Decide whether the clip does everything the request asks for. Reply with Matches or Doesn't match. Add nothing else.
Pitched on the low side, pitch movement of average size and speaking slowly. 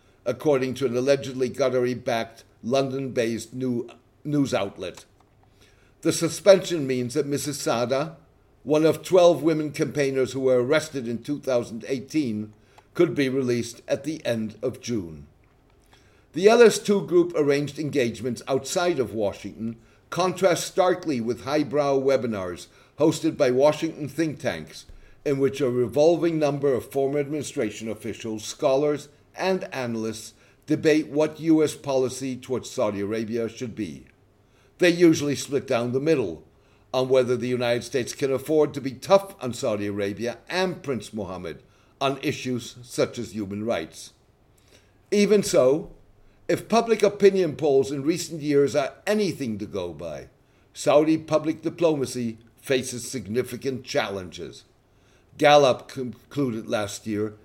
Matches